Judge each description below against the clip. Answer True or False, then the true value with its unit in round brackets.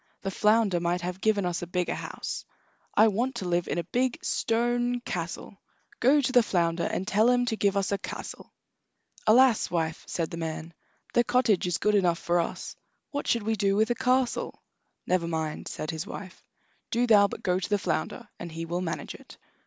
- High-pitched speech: True (195 Hz)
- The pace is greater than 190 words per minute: True (200 wpm)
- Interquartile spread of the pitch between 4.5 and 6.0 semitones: True (5.0 semitones)